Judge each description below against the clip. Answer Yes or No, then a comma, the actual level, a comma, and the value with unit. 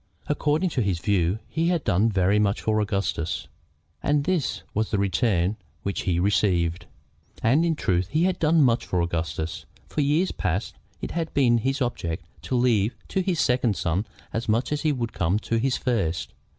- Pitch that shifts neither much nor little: No, wide, 7.4 semitones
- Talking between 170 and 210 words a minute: Yes, average, 180 wpm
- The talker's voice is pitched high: No, low, 110 Hz